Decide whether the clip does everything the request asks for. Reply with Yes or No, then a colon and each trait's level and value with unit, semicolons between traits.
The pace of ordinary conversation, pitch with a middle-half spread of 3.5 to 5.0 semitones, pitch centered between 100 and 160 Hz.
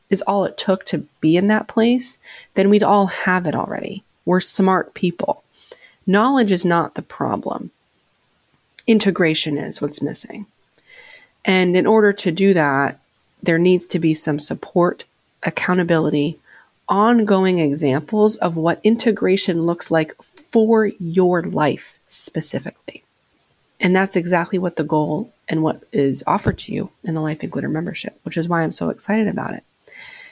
No: average, 150 wpm; average, 4.2 semitones; medium, 185 Hz